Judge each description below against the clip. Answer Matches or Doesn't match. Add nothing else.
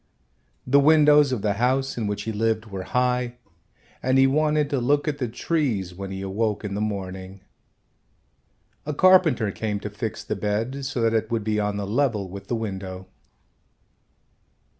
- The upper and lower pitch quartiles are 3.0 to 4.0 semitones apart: Doesn't match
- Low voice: Matches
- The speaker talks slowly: Doesn't match